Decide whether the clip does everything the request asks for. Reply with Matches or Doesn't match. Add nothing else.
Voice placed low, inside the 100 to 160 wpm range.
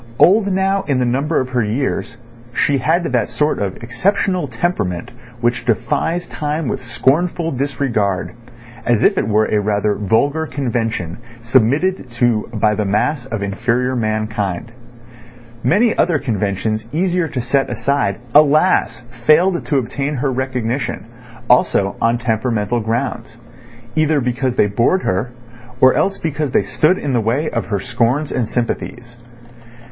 Matches